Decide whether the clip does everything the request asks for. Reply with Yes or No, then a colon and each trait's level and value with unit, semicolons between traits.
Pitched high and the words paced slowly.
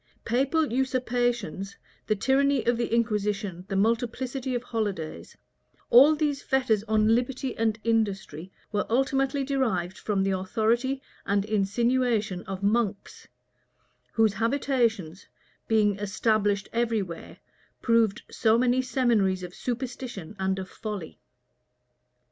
Yes: high, 225 Hz; slow, 115 wpm